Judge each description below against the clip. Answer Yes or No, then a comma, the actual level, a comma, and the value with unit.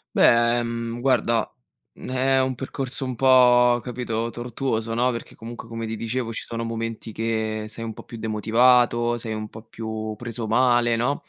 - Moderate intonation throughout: No, narrow, 1.5 semitones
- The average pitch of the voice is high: No, low, 115 Hz